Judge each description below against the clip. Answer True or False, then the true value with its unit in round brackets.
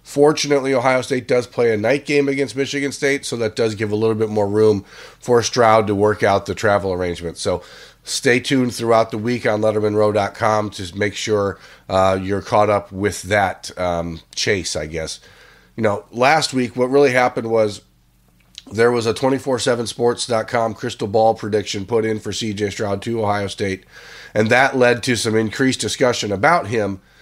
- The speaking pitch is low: True (110 Hz)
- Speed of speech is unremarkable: True (180 wpm)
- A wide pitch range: False (3.5 semitones)